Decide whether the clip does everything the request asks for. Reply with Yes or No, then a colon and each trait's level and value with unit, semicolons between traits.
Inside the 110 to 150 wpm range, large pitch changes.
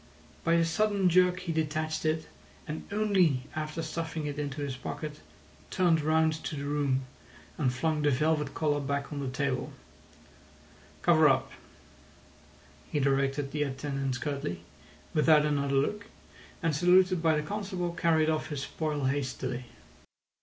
No: average, 145 wpm; average, 2.8 semitones